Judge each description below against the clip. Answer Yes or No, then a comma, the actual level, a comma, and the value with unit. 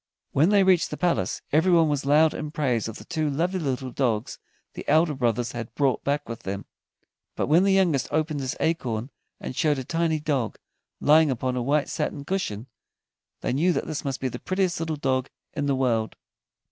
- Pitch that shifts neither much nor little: Yes, average, 4.0 semitones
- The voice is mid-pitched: Yes, medium, 145 Hz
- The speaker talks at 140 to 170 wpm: No, average, 195 wpm